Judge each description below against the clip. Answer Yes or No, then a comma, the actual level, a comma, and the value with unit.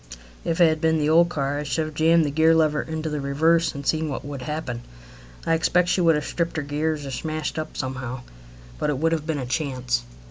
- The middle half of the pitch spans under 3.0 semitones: Yes, narrow, 2.5 semitones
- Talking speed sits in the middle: No, fast, 240 wpm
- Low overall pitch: No, medium, 155 Hz